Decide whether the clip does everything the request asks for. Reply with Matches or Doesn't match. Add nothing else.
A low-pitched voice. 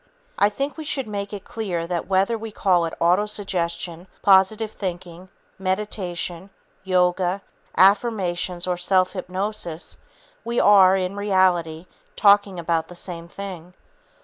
Doesn't match